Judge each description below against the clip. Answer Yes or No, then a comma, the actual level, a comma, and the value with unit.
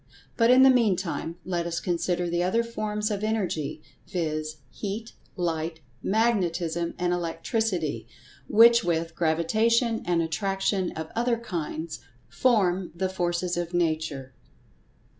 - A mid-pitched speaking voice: Yes, medium, 180 Hz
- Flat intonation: No, average, 4.6 semitones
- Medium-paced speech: No, slow, 120 wpm